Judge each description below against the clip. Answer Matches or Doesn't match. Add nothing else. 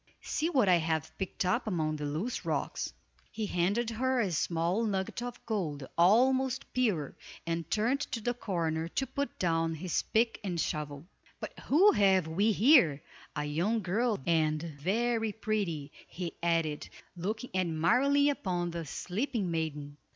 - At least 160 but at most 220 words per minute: Doesn't match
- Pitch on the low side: Doesn't match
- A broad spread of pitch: Matches